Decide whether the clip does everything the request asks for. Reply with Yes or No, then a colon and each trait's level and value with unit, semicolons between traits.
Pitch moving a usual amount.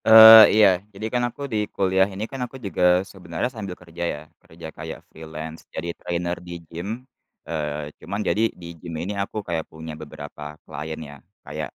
Yes: average, 4.7 semitones